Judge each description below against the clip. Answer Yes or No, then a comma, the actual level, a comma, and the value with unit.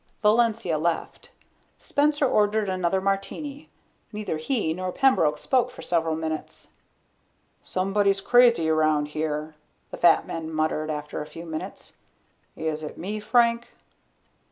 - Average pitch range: No, wide, 5.7 semitones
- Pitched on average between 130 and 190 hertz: Yes, medium, 185 Hz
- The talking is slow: Yes, slow, 125 wpm